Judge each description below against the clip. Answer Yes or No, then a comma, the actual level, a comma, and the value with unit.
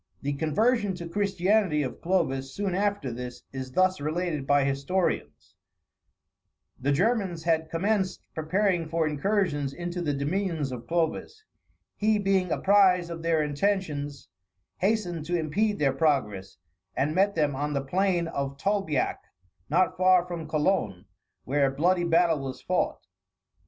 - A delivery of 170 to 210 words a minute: No, average, 140 wpm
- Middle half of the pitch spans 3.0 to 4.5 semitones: No, average, 5.0 semitones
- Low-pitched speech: No, medium, 165 Hz